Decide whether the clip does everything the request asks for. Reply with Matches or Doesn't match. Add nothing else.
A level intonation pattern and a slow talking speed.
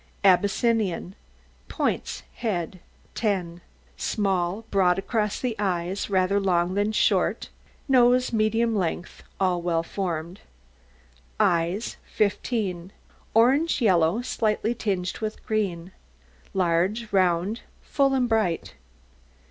Doesn't match